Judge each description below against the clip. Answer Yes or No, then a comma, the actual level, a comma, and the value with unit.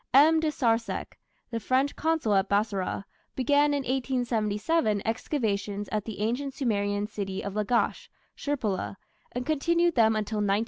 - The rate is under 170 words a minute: Yes, average, 140 wpm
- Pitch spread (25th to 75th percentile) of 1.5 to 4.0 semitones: No, average, 5.2 semitones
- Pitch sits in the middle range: No, high, 230 Hz